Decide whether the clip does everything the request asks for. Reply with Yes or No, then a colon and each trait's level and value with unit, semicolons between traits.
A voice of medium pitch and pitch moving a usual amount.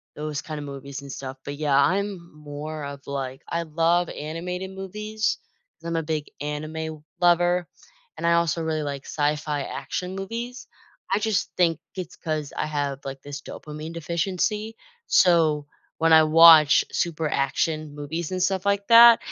Yes: medium, 160 Hz; average, 3.3 semitones